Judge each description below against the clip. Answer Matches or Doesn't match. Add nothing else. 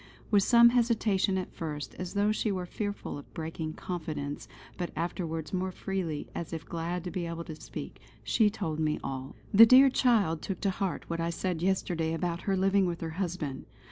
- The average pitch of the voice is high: Doesn't match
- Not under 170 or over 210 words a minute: Matches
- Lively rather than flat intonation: Doesn't match